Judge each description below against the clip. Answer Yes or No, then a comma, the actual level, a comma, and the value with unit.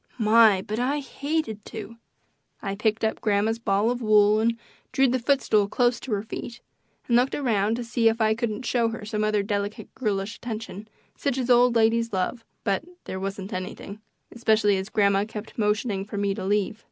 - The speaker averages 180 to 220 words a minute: Yes, average, 190 wpm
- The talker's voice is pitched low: No, high, 220 Hz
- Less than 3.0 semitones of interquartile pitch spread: Yes, narrow, 2.4 semitones